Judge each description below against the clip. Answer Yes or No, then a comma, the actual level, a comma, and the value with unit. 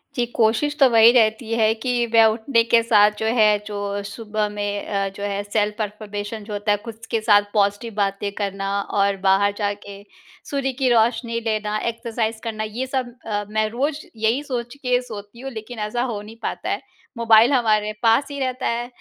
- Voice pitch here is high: Yes, high, 220 Hz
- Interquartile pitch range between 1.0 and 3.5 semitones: Yes, narrow, 2.4 semitones